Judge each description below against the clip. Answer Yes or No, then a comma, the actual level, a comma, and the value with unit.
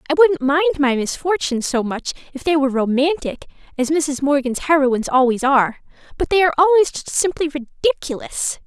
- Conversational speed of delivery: Yes, average, 165 wpm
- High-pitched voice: Yes, very high, 290 Hz